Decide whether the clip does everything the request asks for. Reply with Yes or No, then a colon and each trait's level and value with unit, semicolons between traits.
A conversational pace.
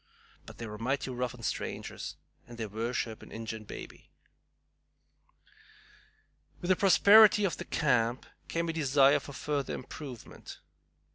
No: slow, 130 wpm